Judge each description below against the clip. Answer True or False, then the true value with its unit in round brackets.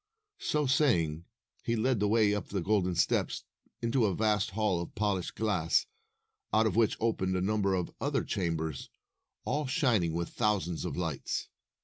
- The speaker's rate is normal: True (160 wpm)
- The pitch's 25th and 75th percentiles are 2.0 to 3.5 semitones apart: False (4.0 semitones)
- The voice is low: True (100 Hz)